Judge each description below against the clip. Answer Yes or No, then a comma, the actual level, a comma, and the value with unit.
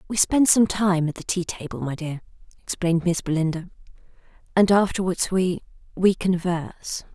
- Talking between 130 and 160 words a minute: Yes, average, 145 wpm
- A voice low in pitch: No, medium, 180 Hz